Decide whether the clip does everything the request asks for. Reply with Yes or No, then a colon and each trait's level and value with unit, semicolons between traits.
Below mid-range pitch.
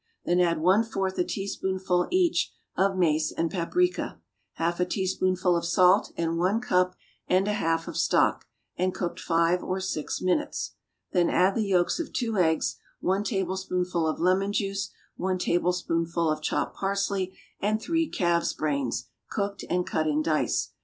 No: medium, 185 Hz